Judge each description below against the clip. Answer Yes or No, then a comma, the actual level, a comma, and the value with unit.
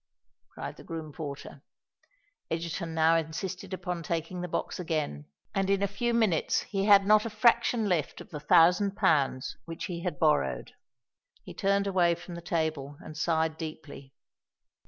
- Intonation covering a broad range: No, average, 3.7 semitones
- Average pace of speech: Yes, average, 160 wpm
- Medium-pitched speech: Yes, medium, 170 Hz